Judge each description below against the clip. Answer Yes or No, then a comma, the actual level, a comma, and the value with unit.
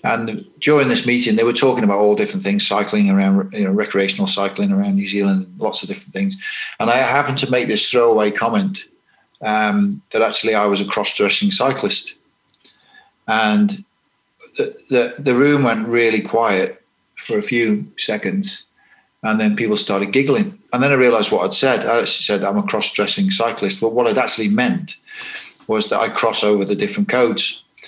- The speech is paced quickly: No, average, 180 wpm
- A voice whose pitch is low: No, medium, 150 Hz